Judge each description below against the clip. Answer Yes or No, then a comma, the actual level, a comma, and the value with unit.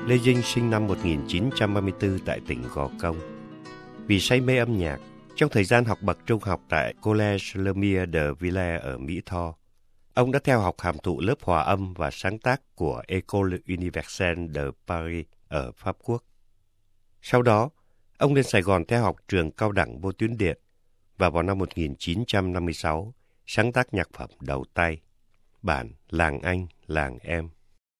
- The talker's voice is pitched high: No, very low, 95 Hz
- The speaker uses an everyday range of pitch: Yes, average, 4.4 semitones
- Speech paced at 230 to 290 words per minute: No, slow, 165 wpm